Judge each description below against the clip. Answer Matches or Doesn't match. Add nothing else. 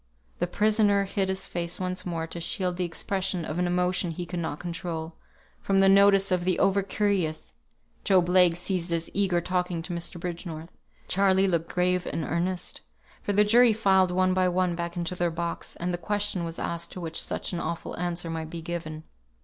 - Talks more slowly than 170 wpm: Doesn't match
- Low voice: Doesn't match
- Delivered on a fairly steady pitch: Matches